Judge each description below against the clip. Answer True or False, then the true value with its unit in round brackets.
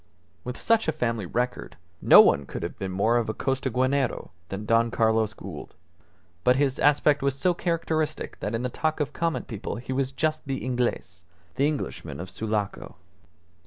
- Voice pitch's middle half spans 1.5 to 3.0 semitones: False (4.8 semitones)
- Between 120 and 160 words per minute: False (170 wpm)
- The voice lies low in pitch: True (125 Hz)